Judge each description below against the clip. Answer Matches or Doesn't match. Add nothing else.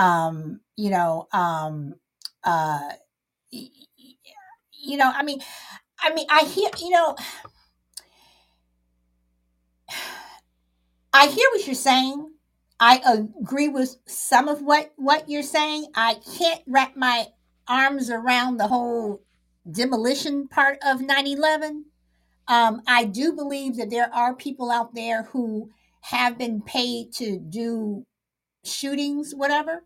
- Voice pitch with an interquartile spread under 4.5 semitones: Doesn't match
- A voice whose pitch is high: Matches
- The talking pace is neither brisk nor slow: Doesn't match